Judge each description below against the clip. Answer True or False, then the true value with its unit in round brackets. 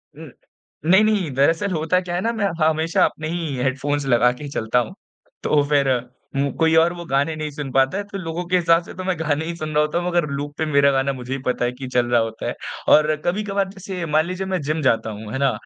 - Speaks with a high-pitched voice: False (155 Hz)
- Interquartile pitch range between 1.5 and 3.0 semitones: False (4.2 semitones)